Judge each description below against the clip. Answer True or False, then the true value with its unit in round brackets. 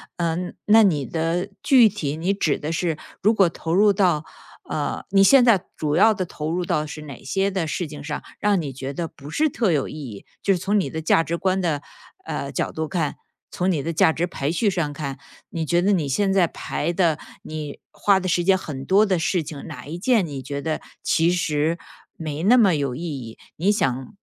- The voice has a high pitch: False (170 Hz)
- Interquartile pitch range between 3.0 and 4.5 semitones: True (4.2 semitones)